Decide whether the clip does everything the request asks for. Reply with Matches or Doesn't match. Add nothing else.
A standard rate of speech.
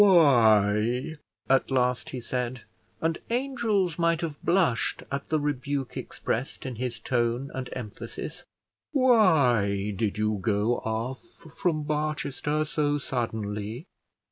Doesn't match